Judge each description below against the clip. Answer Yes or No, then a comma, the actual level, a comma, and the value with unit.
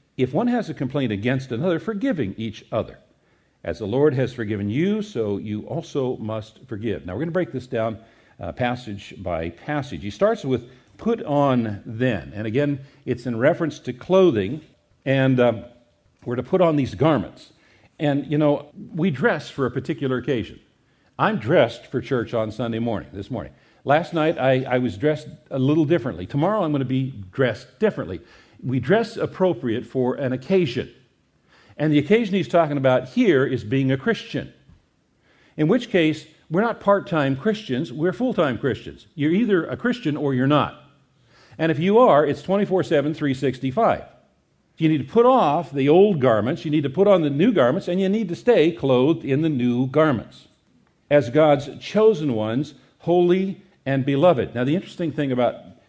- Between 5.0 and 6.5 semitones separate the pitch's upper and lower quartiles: Yes, average, 5.3 semitones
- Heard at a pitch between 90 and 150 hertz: Yes, medium, 140 Hz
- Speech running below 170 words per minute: No, average, 180 wpm